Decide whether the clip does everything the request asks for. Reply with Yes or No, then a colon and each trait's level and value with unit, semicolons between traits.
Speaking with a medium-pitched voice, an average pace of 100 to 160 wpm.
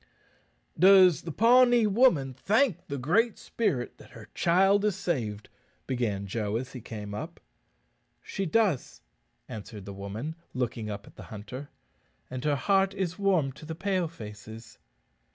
Yes: medium, 150 Hz; average, 150 wpm